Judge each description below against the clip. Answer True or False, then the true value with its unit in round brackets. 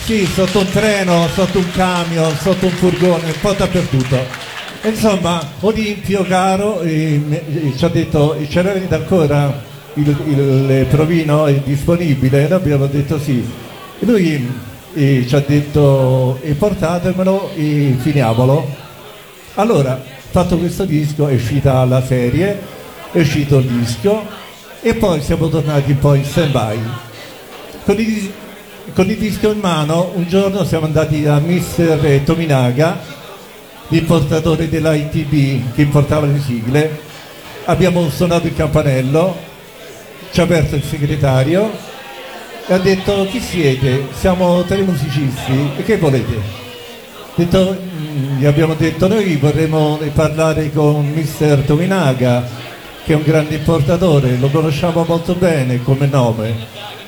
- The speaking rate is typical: True (130 wpm)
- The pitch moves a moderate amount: True (4.2 semitones)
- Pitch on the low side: False (155 Hz)